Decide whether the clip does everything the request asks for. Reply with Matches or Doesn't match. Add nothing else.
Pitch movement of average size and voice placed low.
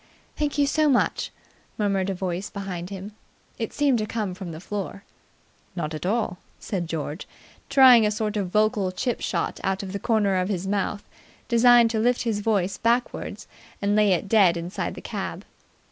Doesn't match